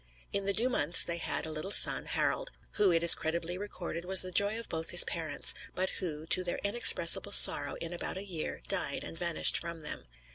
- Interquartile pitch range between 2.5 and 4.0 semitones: Yes, average, 3.0 semitones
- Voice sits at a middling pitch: Yes, medium, 175 Hz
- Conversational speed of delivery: No, fast, 215 wpm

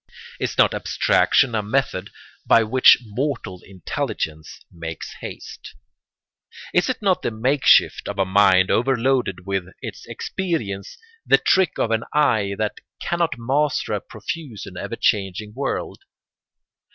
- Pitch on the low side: Yes, low, 110 Hz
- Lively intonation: Yes, wide, 5.7 semitones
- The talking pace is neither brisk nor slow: No, slow, 130 wpm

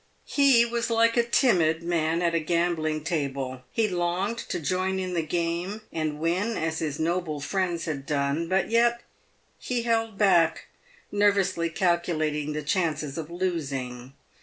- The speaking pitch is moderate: Yes, medium, 170 Hz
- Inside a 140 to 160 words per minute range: Yes, average, 150 wpm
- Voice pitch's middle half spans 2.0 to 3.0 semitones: No, average, 3.9 semitones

